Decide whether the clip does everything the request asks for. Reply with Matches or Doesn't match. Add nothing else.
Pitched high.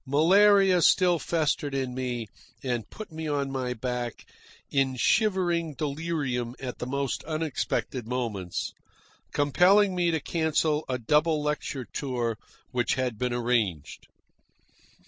Doesn't match